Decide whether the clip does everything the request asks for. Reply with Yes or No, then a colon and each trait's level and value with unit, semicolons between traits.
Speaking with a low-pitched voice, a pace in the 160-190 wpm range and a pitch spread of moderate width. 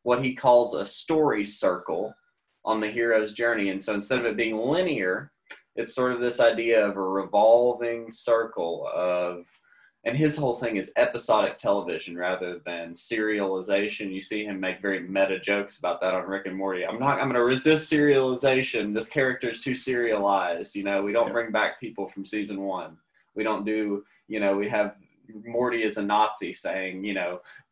Yes: low, 105 Hz; average, 185 wpm; average, 3.5 semitones